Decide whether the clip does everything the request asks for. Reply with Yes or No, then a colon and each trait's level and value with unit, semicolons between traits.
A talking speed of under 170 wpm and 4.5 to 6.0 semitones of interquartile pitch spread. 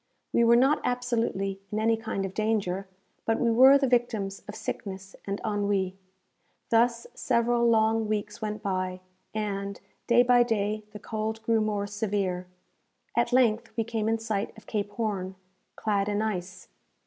No: average, 160 wpm; narrow, 2.6 semitones